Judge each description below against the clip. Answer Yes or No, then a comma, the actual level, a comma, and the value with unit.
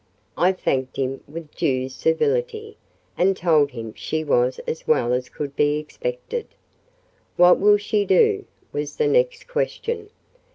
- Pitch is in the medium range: Yes, medium, 180 Hz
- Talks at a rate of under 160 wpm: Yes, average, 140 wpm